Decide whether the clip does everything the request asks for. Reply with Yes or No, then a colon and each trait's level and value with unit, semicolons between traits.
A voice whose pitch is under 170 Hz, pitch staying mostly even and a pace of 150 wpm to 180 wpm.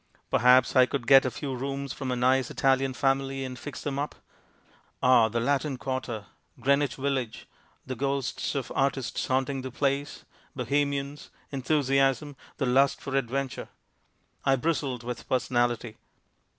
No: low, 135 Hz; narrow, 1.5 semitones; average, 140 wpm